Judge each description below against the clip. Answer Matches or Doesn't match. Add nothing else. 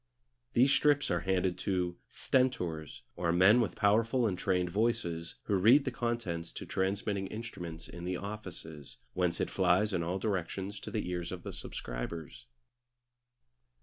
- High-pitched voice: Doesn't match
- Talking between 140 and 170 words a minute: Matches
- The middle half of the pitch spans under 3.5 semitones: Doesn't match